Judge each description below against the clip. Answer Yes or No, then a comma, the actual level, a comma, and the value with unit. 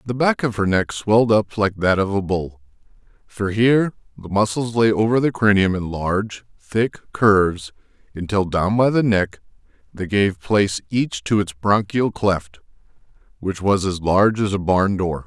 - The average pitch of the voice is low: Yes, low, 100 Hz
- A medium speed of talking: Yes, average, 175 wpm